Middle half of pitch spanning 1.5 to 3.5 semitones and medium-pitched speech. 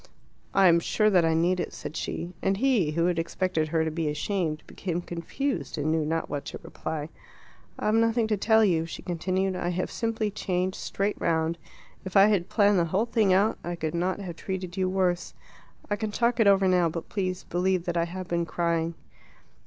Yes: average, 2.9 semitones; medium, 180 Hz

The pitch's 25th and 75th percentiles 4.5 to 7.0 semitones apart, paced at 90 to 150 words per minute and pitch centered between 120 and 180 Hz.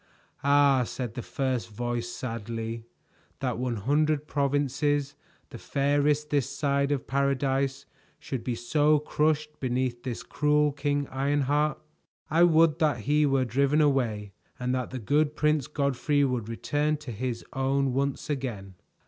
No: average, 2.9 semitones; average, 140 wpm; medium, 140 Hz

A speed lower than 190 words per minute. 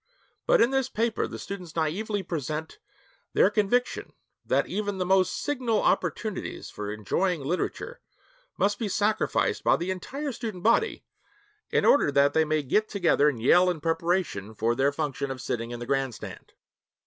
Yes: average, 160 wpm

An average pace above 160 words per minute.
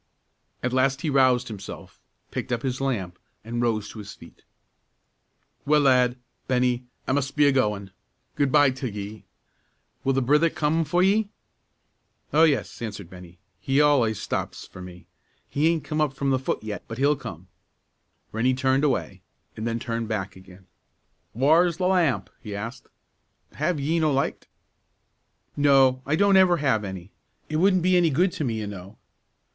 Yes: average, 170 wpm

